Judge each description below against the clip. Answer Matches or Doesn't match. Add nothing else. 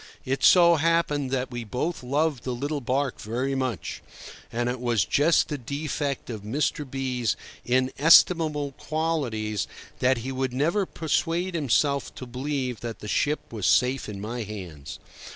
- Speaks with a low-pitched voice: Matches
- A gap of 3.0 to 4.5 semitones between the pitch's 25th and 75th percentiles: Matches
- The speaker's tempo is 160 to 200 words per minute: Doesn't match